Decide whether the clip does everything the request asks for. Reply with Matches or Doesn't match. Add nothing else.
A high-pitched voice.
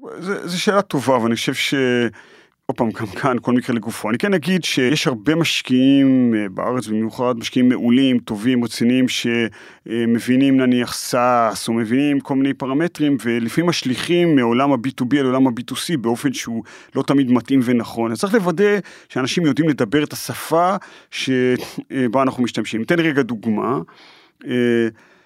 Doesn't match